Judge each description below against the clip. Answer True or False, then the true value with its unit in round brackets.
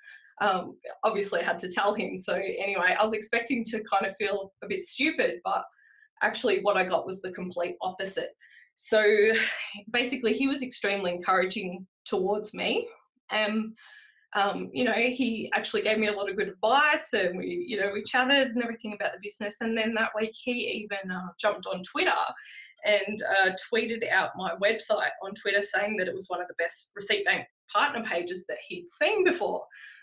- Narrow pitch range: False (4.3 semitones)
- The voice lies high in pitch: True (215 Hz)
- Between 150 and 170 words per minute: False (190 wpm)